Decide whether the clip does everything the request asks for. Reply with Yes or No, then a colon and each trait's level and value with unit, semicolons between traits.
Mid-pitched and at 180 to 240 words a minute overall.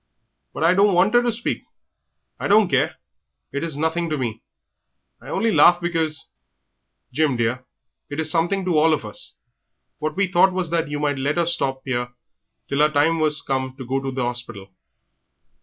Yes: medium, 155 Hz; average, 190 wpm